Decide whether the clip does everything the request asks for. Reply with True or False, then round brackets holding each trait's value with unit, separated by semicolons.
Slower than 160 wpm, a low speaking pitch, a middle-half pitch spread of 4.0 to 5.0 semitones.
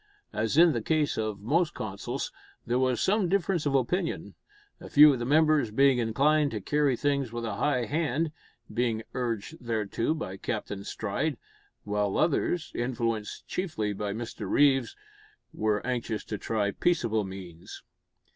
False (150 wpm; 120 Hz; 5.6 semitones)